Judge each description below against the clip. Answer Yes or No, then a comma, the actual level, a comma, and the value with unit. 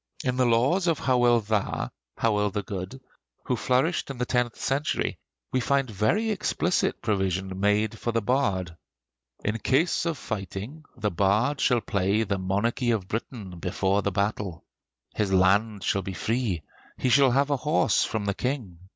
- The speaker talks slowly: No, average, 165 wpm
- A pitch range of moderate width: Yes, average, 4.6 semitones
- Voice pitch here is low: Yes, low, 110 Hz